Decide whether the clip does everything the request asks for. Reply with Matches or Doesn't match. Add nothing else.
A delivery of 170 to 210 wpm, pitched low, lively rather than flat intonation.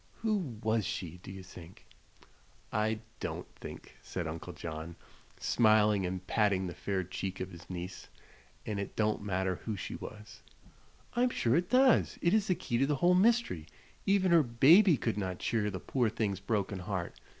Matches